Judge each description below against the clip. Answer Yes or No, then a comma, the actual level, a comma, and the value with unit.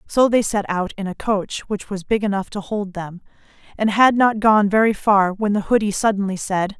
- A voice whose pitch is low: No, high, 205 Hz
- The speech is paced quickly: Yes, fast, 220 wpm